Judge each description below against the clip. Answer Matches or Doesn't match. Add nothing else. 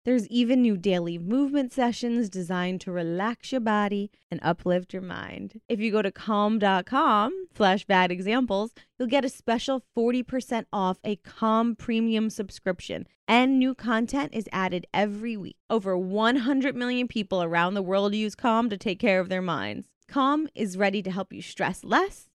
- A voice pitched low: Doesn't match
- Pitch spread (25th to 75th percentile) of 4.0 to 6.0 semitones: Matches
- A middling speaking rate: Matches